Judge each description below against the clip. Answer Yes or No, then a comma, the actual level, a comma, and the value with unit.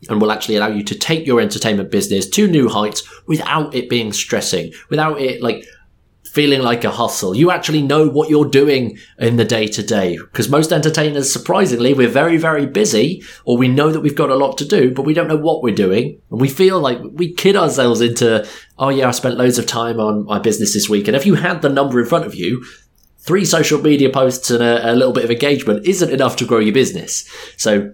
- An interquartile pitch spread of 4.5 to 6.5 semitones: Yes, average, 4.9 semitones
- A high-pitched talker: No, low, 135 Hz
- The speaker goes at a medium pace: No, fast, 230 wpm